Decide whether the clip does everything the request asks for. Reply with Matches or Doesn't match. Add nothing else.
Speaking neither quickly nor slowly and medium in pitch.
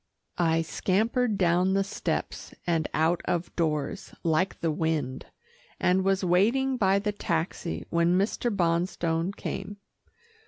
Doesn't match